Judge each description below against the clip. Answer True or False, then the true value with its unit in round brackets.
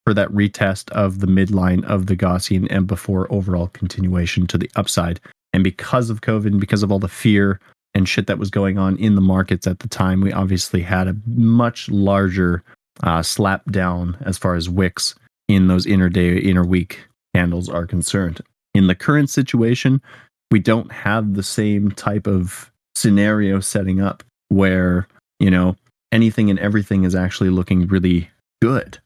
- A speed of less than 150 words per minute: False (175 wpm)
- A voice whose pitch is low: True (95 Hz)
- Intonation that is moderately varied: False (2.2 semitones)